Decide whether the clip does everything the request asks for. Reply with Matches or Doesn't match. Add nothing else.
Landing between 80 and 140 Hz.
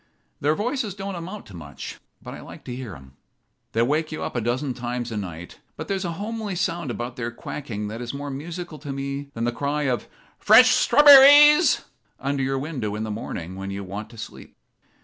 Matches